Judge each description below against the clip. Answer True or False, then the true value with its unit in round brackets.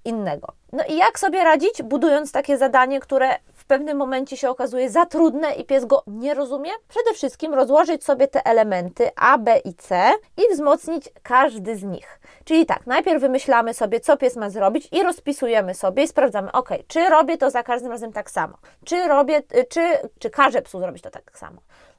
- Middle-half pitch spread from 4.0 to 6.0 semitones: True (4.5 semitones)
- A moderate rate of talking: False (190 wpm)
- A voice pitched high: True (275 Hz)